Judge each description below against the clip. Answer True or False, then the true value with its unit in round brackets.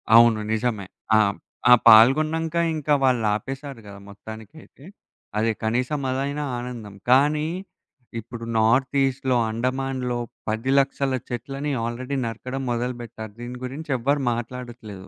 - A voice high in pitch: False (125 Hz)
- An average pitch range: True (3.1 semitones)